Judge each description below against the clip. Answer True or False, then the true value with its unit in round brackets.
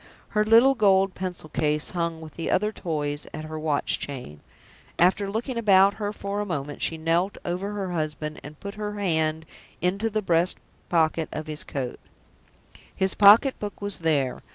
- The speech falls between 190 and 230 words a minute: False (175 wpm)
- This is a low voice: False (175 Hz)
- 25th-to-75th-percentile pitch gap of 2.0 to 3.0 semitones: False (4.6 semitones)